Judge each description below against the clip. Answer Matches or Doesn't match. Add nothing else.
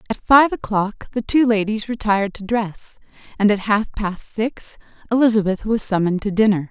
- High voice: Matches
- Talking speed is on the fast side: Doesn't match